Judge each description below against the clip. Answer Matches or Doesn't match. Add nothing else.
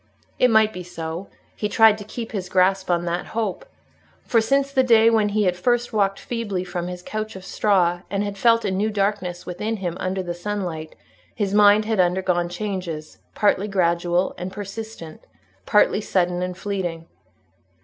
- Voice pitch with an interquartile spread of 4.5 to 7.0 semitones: Doesn't match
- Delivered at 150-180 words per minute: Matches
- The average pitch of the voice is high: Matches